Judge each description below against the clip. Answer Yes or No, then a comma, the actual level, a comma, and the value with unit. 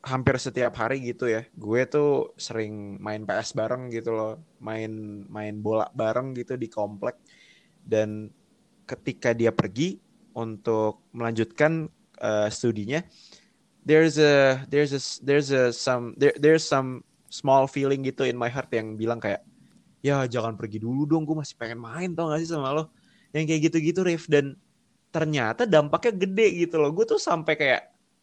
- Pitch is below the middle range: Yes, low, 130 Hz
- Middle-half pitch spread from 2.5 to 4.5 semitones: No, wide, 5.4 semitones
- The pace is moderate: No, fast, 160 wpm